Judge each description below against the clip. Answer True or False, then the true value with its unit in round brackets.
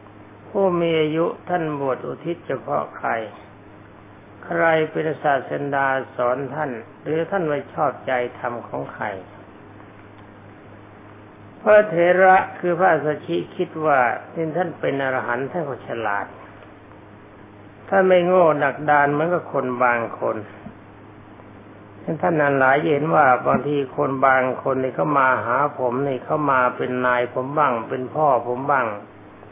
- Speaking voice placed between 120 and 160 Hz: True (130 Hz)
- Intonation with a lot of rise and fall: True (6.6 semitones)